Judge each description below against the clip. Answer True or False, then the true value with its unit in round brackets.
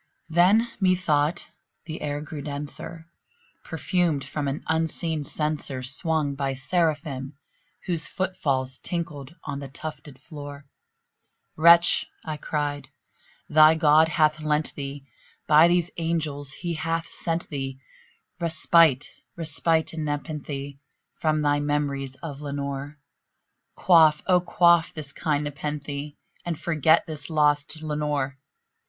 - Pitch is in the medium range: True (150 Hz)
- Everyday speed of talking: False (120 wpm)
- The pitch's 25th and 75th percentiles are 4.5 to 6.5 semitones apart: False (2.4 semitones)